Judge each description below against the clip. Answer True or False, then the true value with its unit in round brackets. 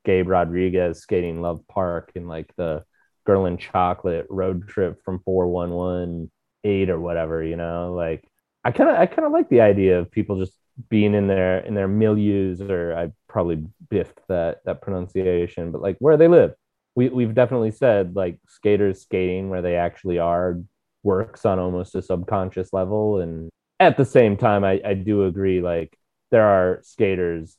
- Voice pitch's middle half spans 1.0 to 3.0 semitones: True (2.6 semitones)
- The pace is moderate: True (175 wpm)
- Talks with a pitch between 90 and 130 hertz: True (95 Hz)